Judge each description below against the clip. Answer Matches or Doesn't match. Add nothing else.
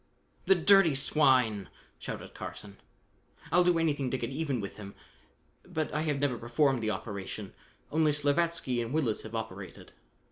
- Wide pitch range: Matches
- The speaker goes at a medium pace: Matches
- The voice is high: Doesn't match